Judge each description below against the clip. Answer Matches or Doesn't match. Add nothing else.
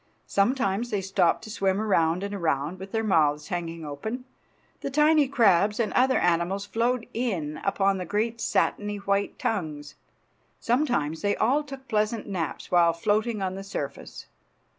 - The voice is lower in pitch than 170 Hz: Doesn't match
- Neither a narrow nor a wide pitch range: Matches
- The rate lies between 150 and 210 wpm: Matches